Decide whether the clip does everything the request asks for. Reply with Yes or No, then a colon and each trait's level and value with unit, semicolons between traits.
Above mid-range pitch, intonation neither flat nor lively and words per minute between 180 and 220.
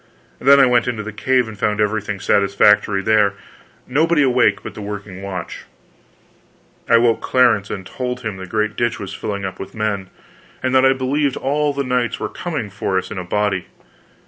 No: low, 110 Hz; average, 4.2 semitones; average, 190 wpm